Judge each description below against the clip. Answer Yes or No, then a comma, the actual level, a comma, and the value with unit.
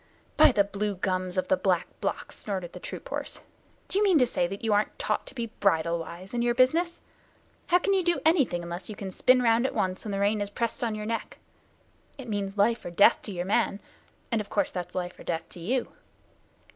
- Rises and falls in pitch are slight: No, average, 4.7 semitones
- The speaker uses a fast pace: Yes, fast, 235 wpm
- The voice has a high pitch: Yes, high, 205 Hz